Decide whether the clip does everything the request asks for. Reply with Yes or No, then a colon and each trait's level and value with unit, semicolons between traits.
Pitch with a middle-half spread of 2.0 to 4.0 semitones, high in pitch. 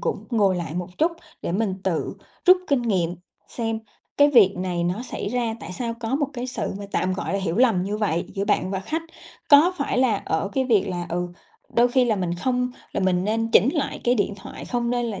No: average, 5.0 semitones; high, 215 Hz